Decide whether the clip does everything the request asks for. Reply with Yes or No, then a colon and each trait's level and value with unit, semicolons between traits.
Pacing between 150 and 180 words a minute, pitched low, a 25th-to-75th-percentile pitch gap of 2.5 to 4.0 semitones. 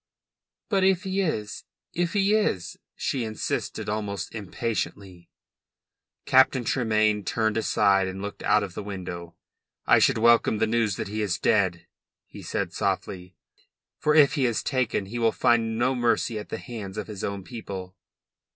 Yes: average, 160 wpm; low, 110 Hz; average, 3.5 semitones